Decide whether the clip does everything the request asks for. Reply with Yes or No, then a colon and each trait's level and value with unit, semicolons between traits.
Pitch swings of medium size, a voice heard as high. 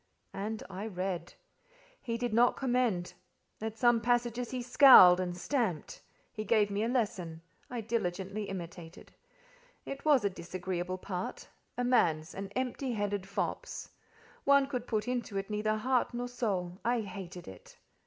Yes: average, 4.8 semitones; high, 215 Hz